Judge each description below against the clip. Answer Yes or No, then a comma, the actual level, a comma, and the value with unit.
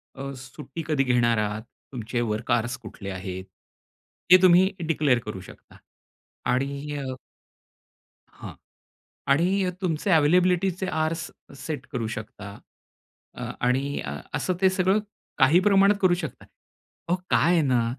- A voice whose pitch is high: No, medium, 145 Hz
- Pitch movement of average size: No, wide, 6.6 semitones